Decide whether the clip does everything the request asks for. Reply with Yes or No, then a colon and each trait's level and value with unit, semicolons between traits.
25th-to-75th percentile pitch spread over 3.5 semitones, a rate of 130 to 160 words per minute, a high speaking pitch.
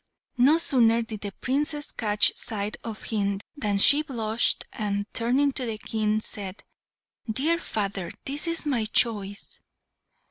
Yes: average, 4.7 semitones; average, 140 wpm; high, 225 Hz